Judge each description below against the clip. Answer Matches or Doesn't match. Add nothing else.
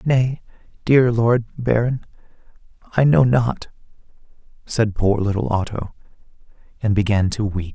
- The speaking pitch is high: Doesn't match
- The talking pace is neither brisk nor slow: Doesn't match